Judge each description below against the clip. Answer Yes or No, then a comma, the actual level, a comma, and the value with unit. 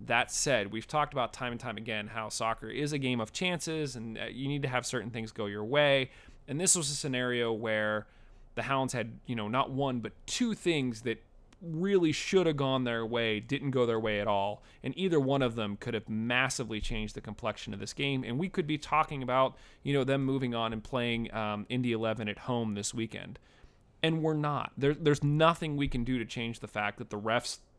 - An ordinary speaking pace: No, fast, 225 wpm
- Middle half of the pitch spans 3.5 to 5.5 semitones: Yes, average, 4.1 semitones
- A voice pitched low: Yes, low, 125 Hz